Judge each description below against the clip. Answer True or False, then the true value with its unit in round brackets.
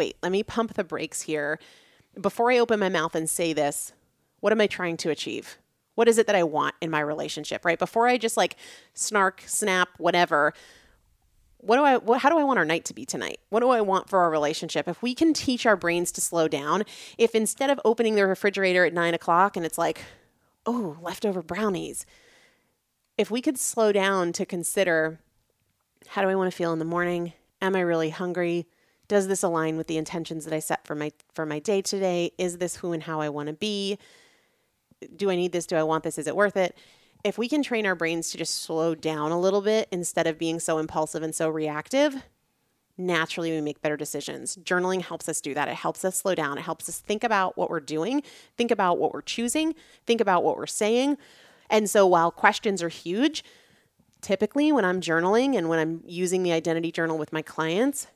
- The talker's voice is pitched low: False (180 Hz)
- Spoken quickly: True (220 wpm)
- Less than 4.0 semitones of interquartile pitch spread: False (4.7 semitones)